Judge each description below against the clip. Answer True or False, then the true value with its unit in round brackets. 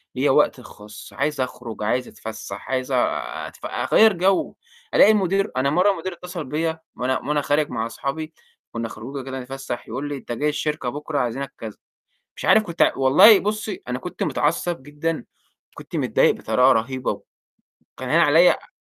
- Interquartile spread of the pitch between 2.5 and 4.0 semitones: False (4.7 semitones)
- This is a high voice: False (140 Hz)